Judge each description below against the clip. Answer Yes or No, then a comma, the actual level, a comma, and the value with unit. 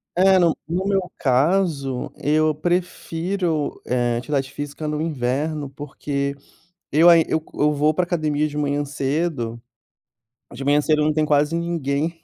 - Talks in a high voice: No, medium, 150 Hz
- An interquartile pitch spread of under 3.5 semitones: Yes, average, 2.9 semitones